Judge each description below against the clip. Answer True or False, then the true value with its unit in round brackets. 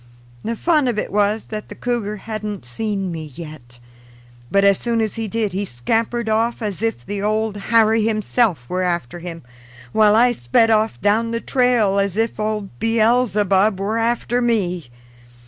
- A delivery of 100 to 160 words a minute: False (170 wpm)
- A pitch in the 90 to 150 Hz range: False (215 Hz)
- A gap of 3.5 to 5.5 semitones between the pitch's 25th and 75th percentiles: False (2.8 semitones)